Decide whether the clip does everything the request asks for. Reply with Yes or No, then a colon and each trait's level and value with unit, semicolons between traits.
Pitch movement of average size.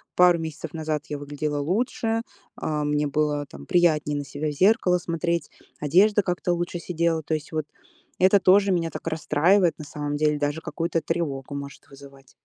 Yes: average, 3.1 semitones